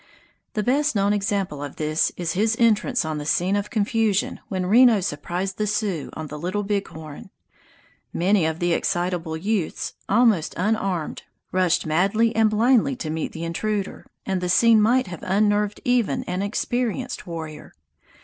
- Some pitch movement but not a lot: Yes, average, 4.2 semitones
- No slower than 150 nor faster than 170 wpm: Yes, average, 160 wpm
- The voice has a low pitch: No, high, 195 Hz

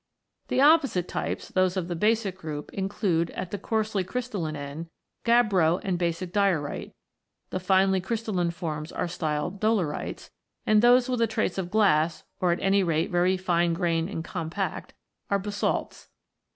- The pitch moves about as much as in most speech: Yes, average, 3.6 semitones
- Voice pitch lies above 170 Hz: Yes, medium, 185 Hz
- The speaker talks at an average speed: Yes, average, 155 wpm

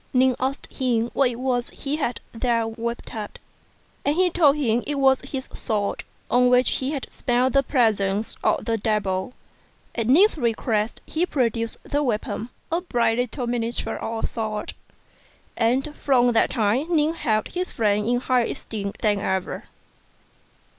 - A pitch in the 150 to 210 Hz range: No, high, 245 Hz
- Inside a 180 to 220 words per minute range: No, average, 165 wpm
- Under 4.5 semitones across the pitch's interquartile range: Yes, average, 3.1 semitones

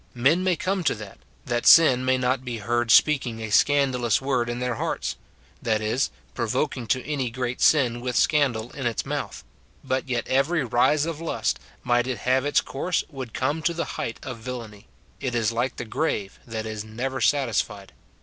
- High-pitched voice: No, low, 125 Hz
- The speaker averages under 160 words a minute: No, average, 200 wpm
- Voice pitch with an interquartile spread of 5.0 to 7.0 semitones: No, average, 3.0 semitones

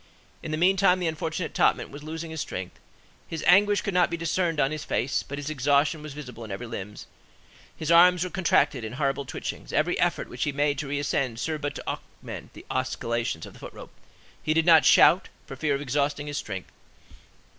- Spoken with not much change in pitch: No, average, 3.4 semitones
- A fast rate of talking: Yes, fast, 210 wpm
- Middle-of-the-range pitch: Yes, medium, 150 Hz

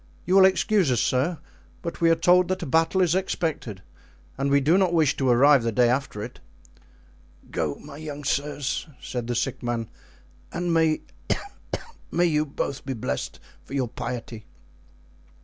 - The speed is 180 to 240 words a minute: No, average, 165 wpm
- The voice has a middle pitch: Yes, medium, 145 Hz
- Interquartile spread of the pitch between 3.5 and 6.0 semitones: Yes, average, 5.1 semitones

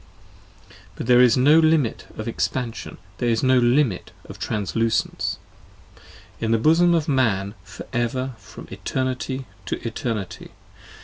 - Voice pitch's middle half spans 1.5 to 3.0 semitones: Yes, average, 2.7 semitones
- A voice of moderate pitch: No, low, 125 Hz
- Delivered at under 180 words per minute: Yes, slow, 135 wpm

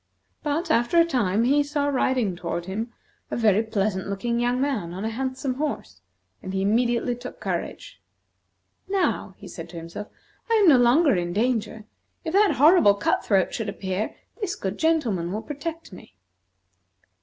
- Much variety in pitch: Yes, wide, 6.4 semitones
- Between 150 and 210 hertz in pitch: No, high, 235 Hz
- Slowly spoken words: No, average, 165 wpm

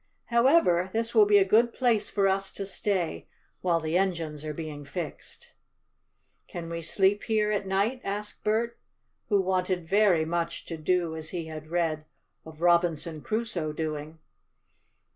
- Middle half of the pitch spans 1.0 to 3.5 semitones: No, average, 4.4 semitones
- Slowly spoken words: No, average, 155 wpm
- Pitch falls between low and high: Yes, medium, 180 Hz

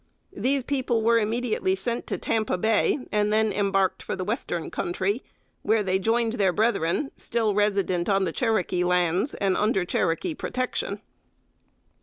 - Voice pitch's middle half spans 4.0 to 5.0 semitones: No, average, 3.6 semitones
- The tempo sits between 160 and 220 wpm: No, average, 150 wpm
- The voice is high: Yes, high, 210 Hz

